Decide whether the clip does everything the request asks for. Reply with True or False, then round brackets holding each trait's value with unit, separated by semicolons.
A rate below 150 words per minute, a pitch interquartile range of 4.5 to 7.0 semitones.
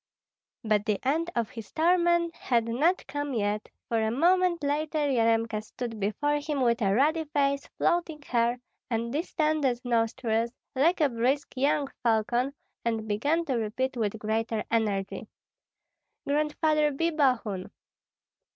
True (135 wpm; 5.0 semitones)